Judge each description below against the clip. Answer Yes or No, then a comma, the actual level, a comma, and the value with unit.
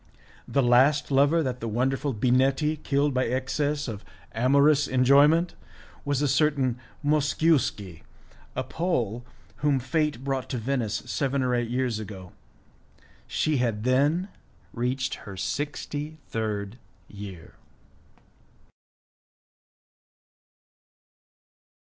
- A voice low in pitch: Yes, low, 130 Hz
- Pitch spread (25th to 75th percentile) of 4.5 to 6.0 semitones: No, average, 3.3 semitones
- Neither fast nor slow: No, slow, 100 wpm